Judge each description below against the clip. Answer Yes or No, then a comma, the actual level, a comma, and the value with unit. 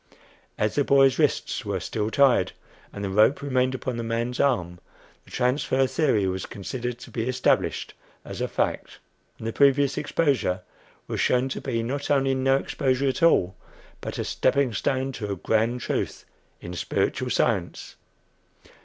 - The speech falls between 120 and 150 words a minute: No, average, 160 wpm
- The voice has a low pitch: Yes, low, 125 Hz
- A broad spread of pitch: No, average, 3.6 semitones